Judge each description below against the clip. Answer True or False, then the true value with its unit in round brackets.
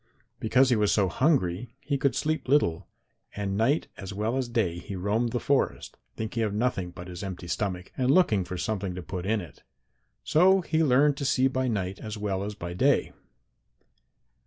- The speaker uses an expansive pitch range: True (5.7 semitones)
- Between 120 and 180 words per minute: False (190 wpm)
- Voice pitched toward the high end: False (110 Hz)